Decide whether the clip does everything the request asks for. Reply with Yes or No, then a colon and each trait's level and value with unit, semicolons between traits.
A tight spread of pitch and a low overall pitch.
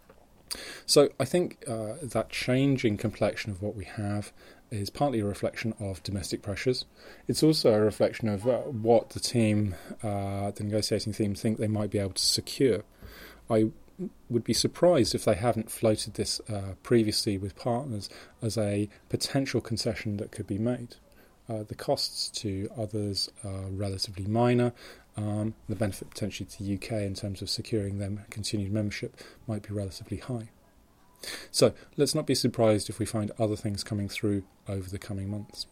Yes: narrow, 2.3 semitones; low, 110 Hz